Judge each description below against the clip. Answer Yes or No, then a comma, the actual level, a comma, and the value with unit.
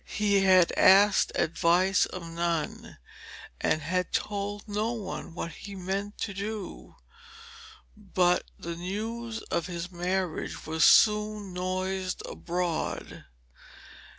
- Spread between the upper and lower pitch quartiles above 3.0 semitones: No, average, 2.7 semitones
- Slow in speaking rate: Yes, slow, 110 wpm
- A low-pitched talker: No, medium, 185 Hz